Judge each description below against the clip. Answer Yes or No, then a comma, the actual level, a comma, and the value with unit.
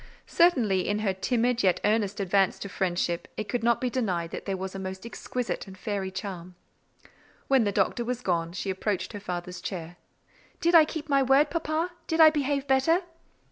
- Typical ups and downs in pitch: No, wide, 6.0 semitones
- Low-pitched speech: No, high, 210 Hz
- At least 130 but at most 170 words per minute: No, average, 190 wpm